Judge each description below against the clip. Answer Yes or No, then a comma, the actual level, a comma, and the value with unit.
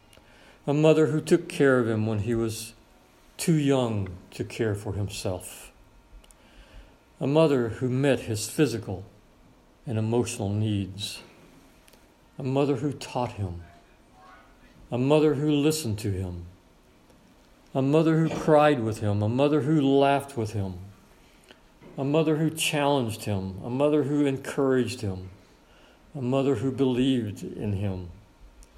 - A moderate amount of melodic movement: No, wide, 5.8 semitones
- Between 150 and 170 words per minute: No, slow, 135 wpm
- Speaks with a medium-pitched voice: No, low, 120 Hz